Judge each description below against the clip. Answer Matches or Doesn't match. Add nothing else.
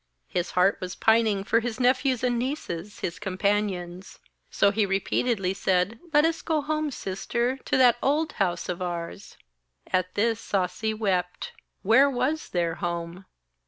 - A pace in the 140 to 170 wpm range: Matches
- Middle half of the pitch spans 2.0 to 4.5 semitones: Doesn't match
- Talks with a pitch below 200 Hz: Doesn't match